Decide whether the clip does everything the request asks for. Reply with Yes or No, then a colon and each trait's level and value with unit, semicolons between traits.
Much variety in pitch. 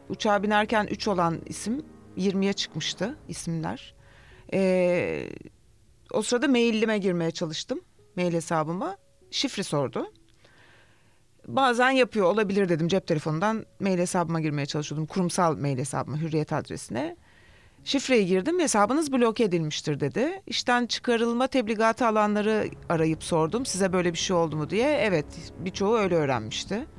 Yes: wide, 6.3 semitones